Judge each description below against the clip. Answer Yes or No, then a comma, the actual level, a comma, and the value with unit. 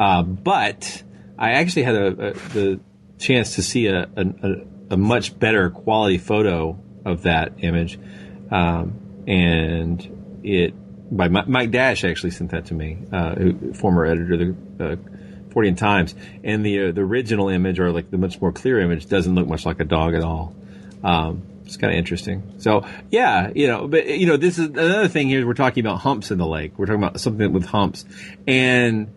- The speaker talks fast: No, average, 195 wpm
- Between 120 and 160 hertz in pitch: No, very low, 95 Hz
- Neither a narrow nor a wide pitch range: Yes, average, 3.3 semitones